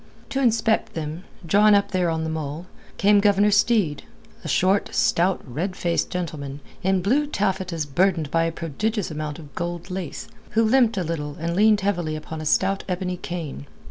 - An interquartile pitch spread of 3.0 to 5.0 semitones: Yes, average, 4.0 semitones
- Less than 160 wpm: No, average, 175 wpm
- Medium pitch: Yes, medium, 180 Hz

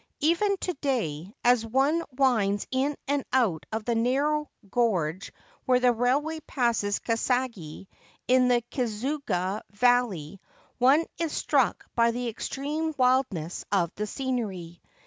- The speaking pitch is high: Yes, high, 245 Hz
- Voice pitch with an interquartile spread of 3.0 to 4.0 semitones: No, average, 4.8 semitones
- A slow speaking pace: Yes, slow, 125 wpm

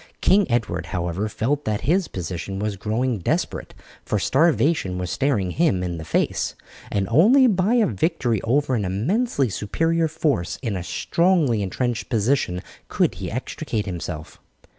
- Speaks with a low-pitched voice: Yes, low, 115 Hz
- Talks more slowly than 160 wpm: Yes, average, 150 wpm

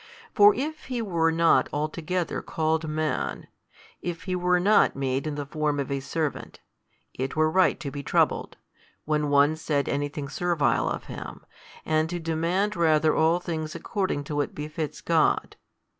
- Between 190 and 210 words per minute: No, average, 165 wpm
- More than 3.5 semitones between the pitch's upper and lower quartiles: No, average, 2.9 semitones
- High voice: No, medium, 155 Hz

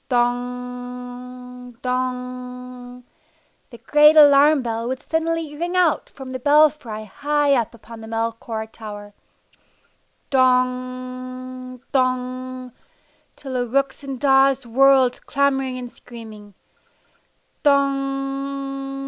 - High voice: Yes, very high, 255 Hz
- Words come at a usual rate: No, slow, 100 wpm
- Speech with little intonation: Yes, narrow, 1.8 semitones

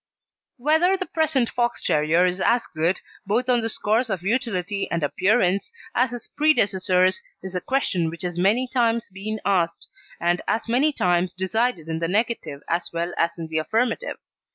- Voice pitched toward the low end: No, high, 195 Hz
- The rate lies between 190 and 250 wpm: No, average, 175 wpm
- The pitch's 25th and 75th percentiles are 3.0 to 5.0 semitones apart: No, wide, 5.5 semitones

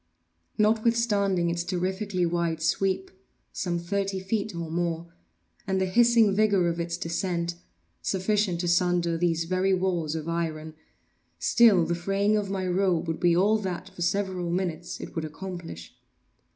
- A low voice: No, medium, 180 Hz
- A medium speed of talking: Yes, average, 150 wpm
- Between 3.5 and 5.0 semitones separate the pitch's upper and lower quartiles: No, narrow, 2.5 semitones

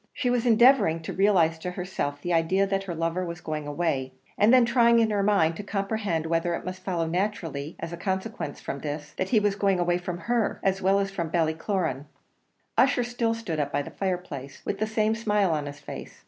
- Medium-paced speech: No, fast, 215 wpm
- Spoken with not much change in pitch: No, average, 4.3 semitones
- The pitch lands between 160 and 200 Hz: Yes, medium, 185 Hz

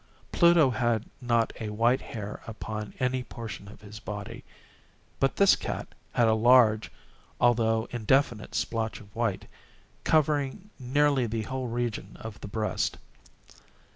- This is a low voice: Yes, low, 115 Hz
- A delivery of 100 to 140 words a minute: Yes, slow, 135 wpm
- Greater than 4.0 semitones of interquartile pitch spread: No, average, 3.1 semitones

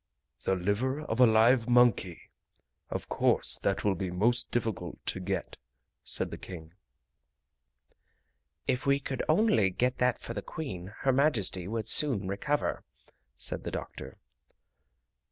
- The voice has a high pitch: No, low, 115 Hz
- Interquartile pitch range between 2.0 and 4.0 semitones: No, average, 5.2 semitones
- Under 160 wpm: Yes, slow, 135 wpm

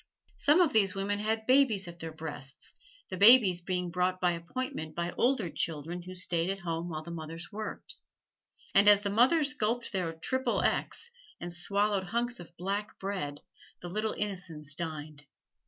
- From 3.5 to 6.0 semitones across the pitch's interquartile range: Yes, average, 4.2 semitones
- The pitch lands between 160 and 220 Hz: Yes, medium, 185 Hz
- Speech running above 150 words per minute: Yes, average, 170 wpm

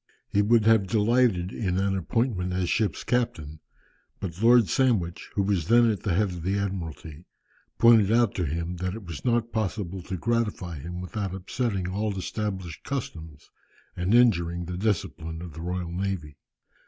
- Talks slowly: No, average, 165 wpm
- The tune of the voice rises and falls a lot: No, average, 4.2 semitones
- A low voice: Yes, very low, 95 Hz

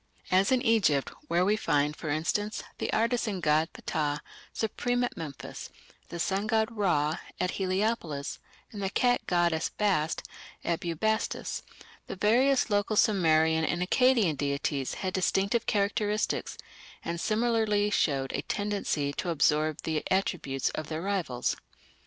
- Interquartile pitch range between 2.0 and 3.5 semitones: No, average, 5.3 semitones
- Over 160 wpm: No, slow, 135 wpm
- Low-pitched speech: No, medium, 185 Hz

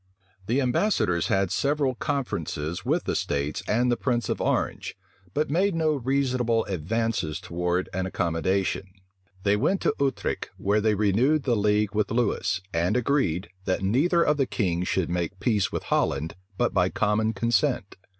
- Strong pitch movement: Yes, wide, 5.7 semitones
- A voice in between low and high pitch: No, low, 105 Hz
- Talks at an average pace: Yes, average, 160 wpm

